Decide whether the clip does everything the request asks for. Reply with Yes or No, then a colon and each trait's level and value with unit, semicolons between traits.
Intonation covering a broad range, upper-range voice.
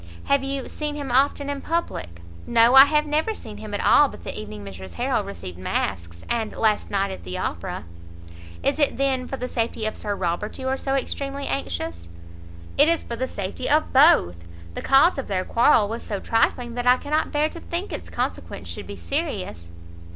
Yes: wide, 7.3 semitones; high, 240 Hz